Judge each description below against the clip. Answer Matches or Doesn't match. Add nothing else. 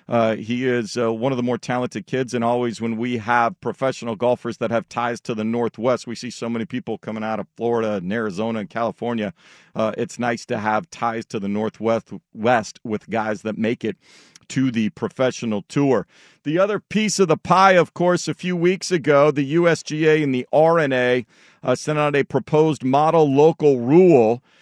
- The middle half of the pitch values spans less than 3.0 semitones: Doesn't match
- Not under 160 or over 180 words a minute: Doesn't match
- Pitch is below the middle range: Matches